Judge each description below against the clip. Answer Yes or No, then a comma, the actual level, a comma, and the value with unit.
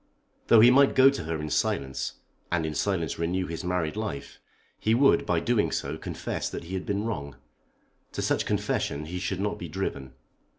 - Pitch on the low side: Yes, very low, 90 Hz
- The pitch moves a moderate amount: Yes, average, 5.0 semitones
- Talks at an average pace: Yes, average, 195 wpm